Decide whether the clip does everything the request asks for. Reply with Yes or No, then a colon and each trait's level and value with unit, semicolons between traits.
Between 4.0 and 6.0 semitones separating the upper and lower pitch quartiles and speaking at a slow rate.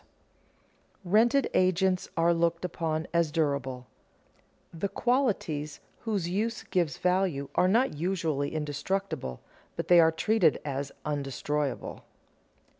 Yes: average, 4.4 semitones; slow, 115 wpm